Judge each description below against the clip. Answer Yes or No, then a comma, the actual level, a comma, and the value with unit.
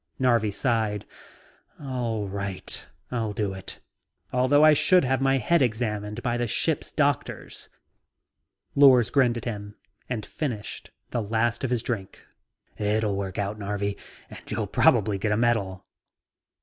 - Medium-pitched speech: No, low, 115 Hz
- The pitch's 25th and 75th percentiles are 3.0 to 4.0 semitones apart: Yes, average, 3.5 semitones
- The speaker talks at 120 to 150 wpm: Yes, average, 140 wpm